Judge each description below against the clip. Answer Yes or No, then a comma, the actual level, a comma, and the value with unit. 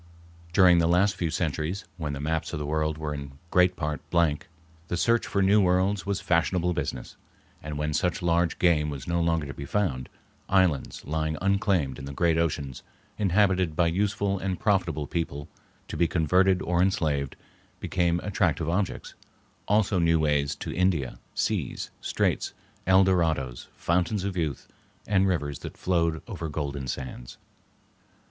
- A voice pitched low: Yes, very low, 85 Hz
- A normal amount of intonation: Yes, average, 3.6 semitones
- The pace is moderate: Yes, average, 160 wpm